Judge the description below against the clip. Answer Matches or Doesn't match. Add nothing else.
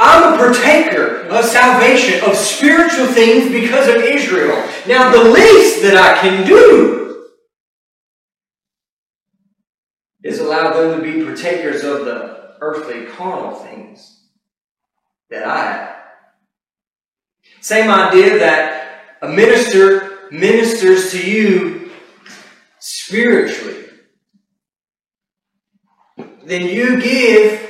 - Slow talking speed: Matches